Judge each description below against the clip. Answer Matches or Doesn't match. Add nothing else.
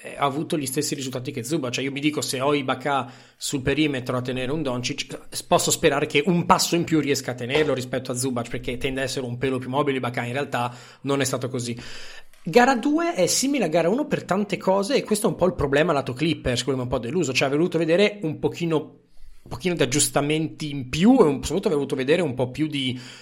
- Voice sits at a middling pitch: Matches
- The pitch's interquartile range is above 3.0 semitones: Matches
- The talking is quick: Matches